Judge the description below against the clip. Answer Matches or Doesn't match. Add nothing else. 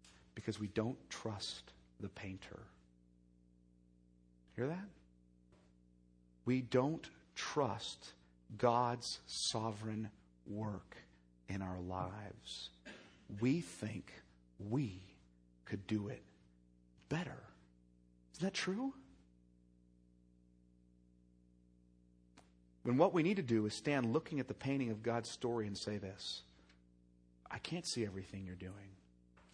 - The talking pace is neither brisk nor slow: Doesn't match